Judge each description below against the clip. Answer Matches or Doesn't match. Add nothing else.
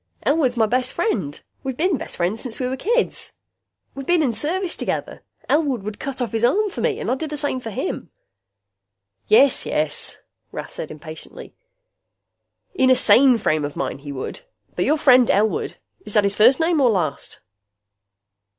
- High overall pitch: Matches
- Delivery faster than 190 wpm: Doesn't match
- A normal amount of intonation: Doesn't match